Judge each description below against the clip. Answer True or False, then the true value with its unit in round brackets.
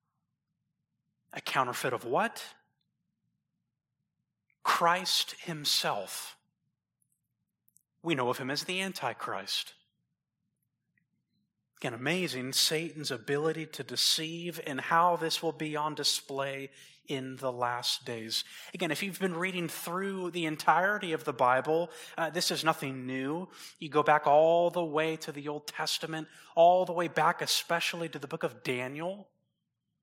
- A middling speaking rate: False (130 wpm)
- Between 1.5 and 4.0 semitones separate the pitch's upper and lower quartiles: True (3.5 semitones)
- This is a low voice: False (155 Hz)